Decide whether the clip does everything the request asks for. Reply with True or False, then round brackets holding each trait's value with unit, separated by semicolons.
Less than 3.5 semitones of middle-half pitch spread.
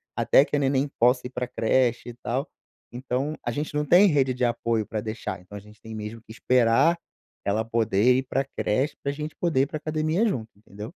False (4.2 semitones)